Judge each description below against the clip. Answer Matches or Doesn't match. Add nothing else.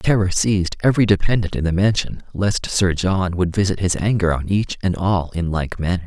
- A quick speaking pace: Matches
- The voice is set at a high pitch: Doesn't match